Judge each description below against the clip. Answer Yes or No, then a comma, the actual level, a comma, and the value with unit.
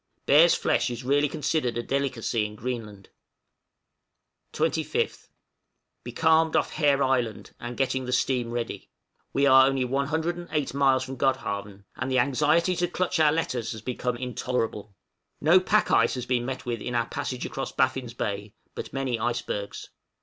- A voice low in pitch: Yes, low, 130 Hz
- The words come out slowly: No, average, 155 wpm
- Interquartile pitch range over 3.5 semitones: No, average, 3.0 semitones